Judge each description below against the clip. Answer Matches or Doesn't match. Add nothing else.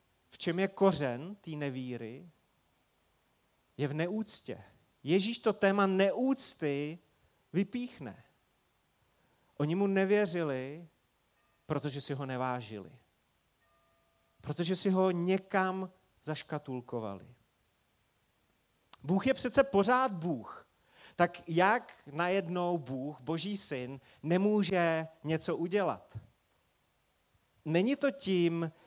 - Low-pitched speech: Doesn't match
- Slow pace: Matches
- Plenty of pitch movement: Matches